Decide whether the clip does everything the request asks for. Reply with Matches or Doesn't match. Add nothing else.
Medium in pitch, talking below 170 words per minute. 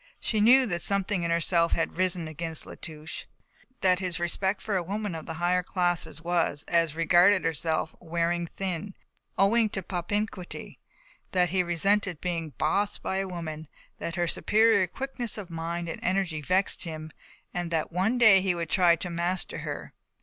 Doesn't match